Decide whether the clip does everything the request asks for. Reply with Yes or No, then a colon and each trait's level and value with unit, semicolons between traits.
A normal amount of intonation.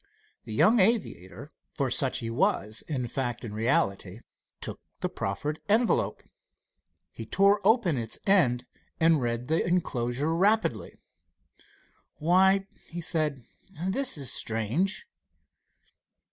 No: wide, 8.2 semitones